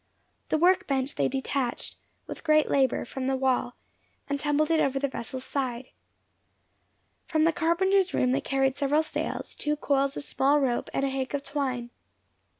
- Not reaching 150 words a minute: No, average, 170 wpm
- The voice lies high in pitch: Yes, very high, 275 Hz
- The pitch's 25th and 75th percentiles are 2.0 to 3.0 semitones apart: Yes, narrow, 2.5 semitones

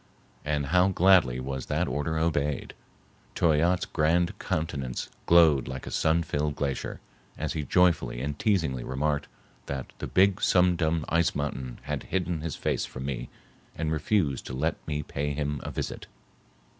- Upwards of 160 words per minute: No, average, 155 wpm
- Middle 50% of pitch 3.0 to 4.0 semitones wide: Yes, average, 3.4 semitones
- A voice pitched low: Yes, very low, 75 Hz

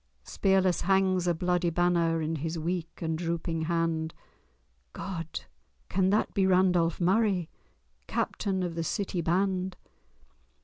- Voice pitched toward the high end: No, medium, 175 Hz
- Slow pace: Yes, slow, 125 wpm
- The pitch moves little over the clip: Yes, narrow, 2.2 semitones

